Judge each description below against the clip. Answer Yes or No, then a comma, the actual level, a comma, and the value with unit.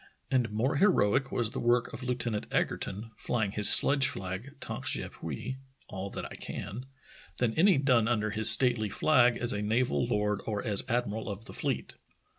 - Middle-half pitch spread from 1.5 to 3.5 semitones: Yes, average, 3.2 semitones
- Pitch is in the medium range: No, low, 115 Hz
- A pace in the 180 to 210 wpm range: Yes, average, 185 wpm